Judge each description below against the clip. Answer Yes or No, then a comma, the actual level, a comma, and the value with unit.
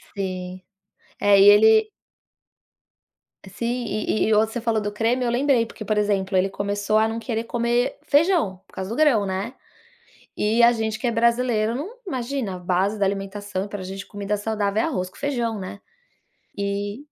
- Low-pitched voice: No, high, 215 Hz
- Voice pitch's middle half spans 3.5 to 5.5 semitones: No, average, 2.9 semitones